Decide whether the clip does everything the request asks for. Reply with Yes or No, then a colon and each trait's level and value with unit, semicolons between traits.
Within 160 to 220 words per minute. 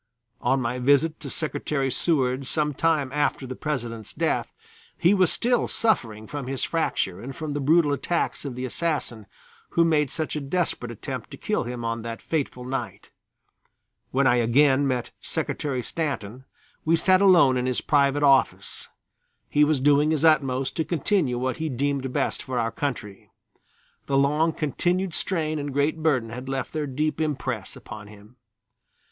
Yes: average, 165 wpm